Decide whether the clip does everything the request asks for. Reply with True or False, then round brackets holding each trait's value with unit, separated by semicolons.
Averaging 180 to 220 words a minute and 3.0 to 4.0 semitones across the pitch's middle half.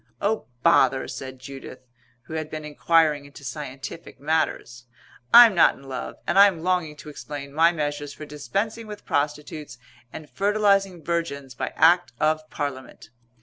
False (145 wpm; 3.6 semitones)